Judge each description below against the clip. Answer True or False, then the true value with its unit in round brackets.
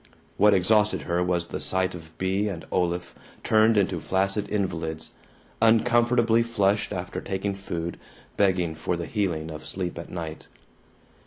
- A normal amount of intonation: True (3.5 semitones)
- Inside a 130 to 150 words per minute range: True (145 wpm)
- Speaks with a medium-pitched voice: False (95 Hz)